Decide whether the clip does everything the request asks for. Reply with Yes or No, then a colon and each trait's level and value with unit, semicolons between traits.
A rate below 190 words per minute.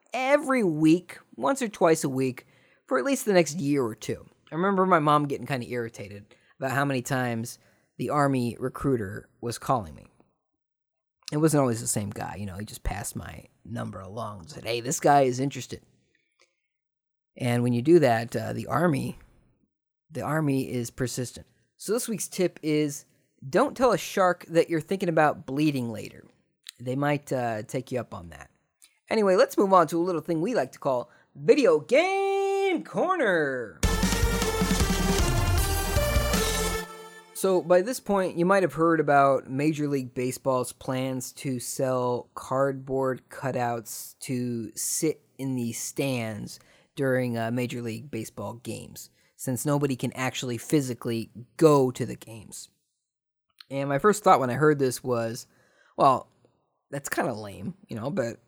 Yes: average, 160 wpm